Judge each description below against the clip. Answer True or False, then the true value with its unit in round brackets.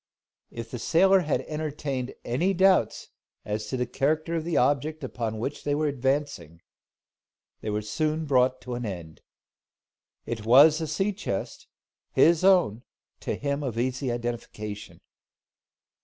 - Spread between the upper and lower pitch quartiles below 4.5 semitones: False (5.0 semitones)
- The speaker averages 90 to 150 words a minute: True (140 wpm)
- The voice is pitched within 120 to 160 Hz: True (135 Hz)